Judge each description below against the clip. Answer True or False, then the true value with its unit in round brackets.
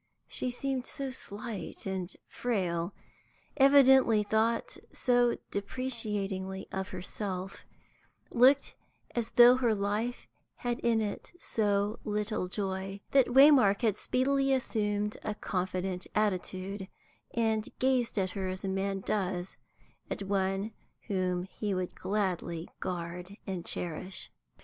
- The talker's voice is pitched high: True (205 Hz)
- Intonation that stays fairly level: False (4.0 semitones)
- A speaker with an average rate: False (115 wpm)